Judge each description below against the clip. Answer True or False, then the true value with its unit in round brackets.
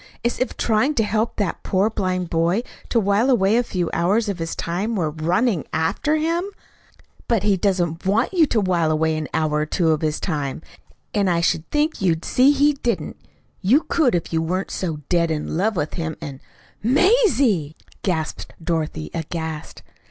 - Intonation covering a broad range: True (6.2 semitones)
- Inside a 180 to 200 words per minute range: True (185 wpm)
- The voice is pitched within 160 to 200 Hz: True (185 Hz)